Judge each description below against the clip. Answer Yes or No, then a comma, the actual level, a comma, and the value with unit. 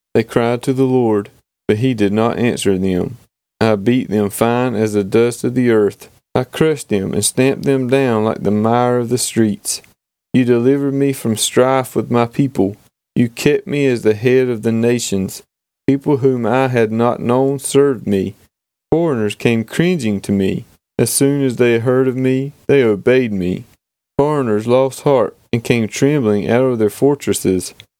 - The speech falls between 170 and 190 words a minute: Yes, average, 180 wpm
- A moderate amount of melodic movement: Yes, average, 3.8 semitones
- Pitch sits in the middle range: No, low, 120 Hz